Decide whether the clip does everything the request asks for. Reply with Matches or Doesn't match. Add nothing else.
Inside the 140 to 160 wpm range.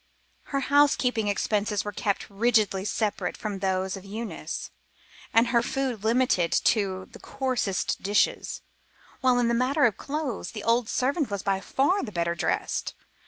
Matches